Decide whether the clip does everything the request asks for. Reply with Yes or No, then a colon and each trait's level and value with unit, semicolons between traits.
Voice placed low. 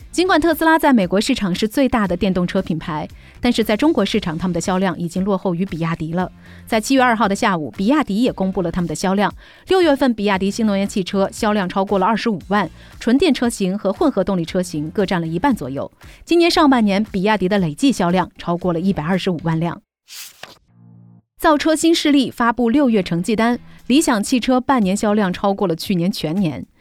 No: high, 200 Hz